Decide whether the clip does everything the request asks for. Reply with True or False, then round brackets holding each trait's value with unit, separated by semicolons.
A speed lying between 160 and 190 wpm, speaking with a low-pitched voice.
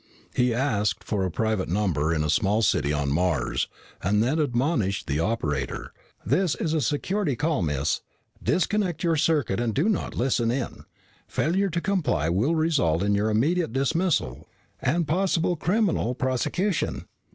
False (150 wpm; 125 Hz)